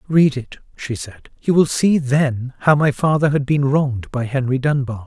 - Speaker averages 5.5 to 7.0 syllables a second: No, 4.6 syllables/s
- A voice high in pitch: No, low, 135 Hz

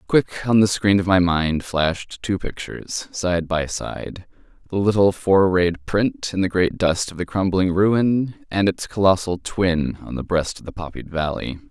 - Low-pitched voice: Yes, very low, 90 Hz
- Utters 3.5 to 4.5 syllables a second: Yes, 4.2 syllables/s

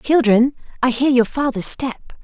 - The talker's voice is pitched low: No, very high, 255 Hz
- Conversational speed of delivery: Yes, average, 160 wpm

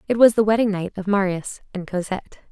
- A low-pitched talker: No, high, 200 Hz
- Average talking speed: No, fast, 215 wpm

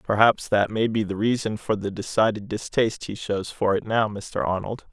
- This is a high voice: No, low, 105 Hz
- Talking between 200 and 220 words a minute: Yes, fast, 205 wpm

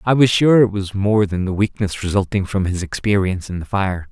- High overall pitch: No, low, 100 Hz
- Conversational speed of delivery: No, fast, 235 wpm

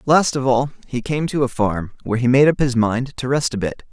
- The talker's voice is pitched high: No, low, 125 Hz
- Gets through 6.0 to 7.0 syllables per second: No, 5.4 syllables/s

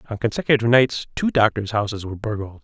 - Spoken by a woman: No, male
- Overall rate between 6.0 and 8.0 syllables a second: Yes, 6.8 syllables/s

